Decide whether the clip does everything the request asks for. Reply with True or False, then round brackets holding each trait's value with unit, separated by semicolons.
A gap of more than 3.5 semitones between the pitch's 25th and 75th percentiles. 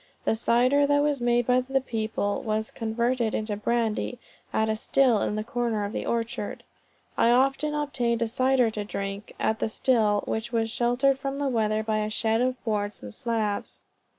False (2.8 semitones)